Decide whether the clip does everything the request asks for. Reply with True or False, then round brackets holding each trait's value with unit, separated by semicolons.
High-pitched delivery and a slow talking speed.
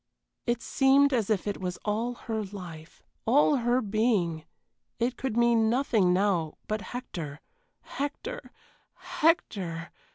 True (220 Hz; 125 wpm)